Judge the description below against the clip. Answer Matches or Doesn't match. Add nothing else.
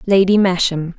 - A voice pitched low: Doesn't match